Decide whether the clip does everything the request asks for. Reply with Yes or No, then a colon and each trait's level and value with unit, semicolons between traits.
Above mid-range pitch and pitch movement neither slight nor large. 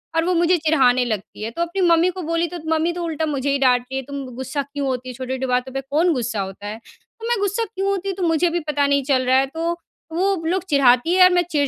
Yes: very high, 295 Hz; average, 4.9 semitones